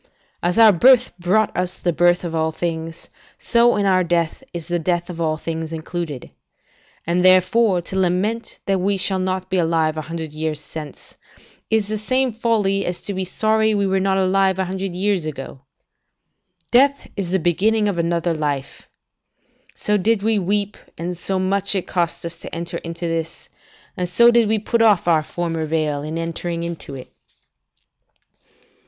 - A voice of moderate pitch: Yes, medium, 180 Hz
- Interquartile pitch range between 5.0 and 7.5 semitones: No, average, 3.3 semitones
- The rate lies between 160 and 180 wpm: Yes, average, 175 wpm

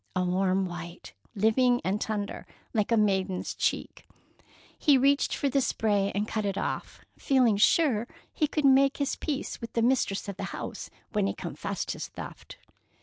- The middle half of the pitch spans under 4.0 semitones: No, average, 5.3 semitones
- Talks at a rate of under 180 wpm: Yes, average, 170 wpm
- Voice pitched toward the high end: Yes, high, 215 Hz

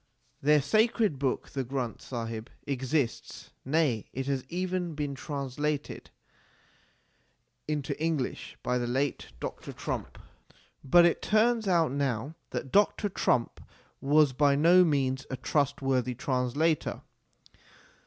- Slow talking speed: Yes, slow, 115 wpm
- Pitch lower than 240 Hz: Yes, medium, 140 Hz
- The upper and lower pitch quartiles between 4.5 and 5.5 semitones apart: No, average, 3.7 semitones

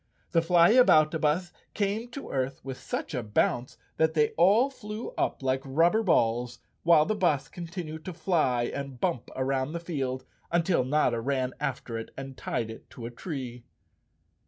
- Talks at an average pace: Yes, average, 160 wpm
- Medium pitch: Yes, medium, 150 Hz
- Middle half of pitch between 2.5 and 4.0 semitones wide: No, average, 5.1 semitones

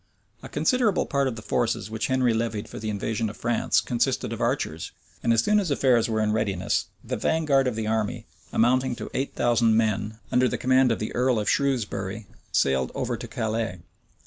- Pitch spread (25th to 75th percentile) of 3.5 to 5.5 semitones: No, average, 3.0 semitones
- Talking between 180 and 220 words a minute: Yes, average, 200 wpm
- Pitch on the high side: No, low, 115 Hz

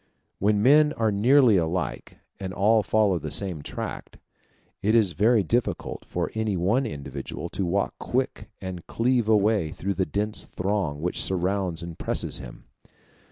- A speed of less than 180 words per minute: Yes, average, 160 wpm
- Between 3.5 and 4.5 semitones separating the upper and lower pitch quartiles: Yes, average, 3.9 semitones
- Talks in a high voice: No, low, 100 Hz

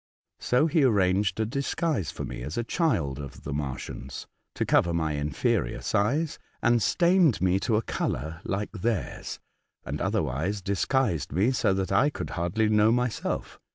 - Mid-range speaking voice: No, low, 100 Hz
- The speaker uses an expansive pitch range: Yes, wide, 7.2 semitones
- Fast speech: No, average, 165 wpm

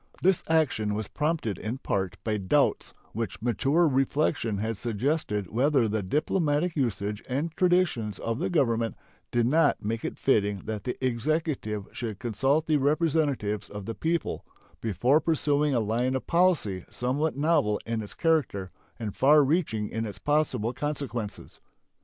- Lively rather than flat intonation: Yes, wide, 6.0 semitones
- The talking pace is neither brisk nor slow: Yes, average, 150 wpm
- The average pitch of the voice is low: Yes, low, 125 Hz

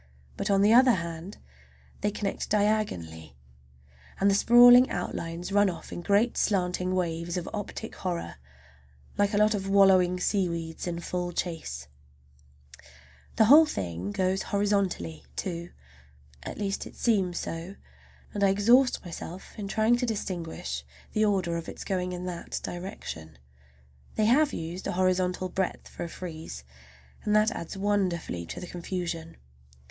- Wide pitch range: No, average, 3.4 semitones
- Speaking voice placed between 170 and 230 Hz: Yes, medium, 185 Hz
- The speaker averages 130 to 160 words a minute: Yes, average, 145 wpm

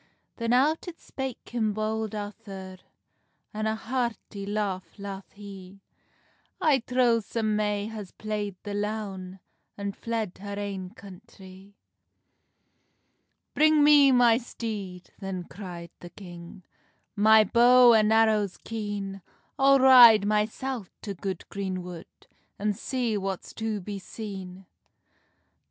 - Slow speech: Yes, slow, 120 wpm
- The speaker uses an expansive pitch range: No, average, 2.9 semitones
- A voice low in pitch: No, high, 210 Hz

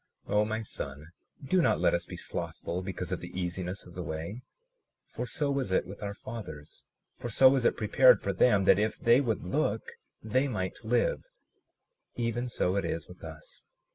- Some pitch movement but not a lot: No, wide, 5.7 semitones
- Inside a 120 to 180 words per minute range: No, average, 195 wpm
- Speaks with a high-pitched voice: No, low, 105 Hz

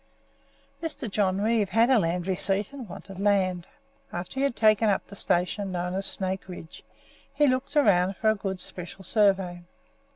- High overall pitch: Yes, high, 195 Hz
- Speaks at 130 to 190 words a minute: Yes, average, 170 wpm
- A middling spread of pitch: Yes, average, 3.2 semitones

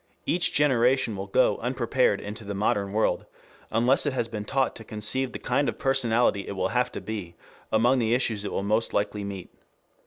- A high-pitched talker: No, low, 115 Hz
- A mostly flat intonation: No, average, 3.7 semitones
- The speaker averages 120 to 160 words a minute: No, average, 195 wpm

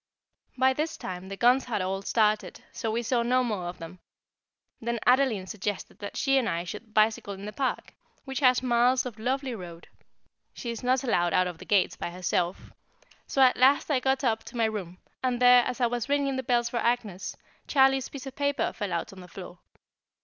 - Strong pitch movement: No, average, 4.9 semitones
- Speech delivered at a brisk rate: Yes, fast, 210 wpm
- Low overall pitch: No, high, 235 Hz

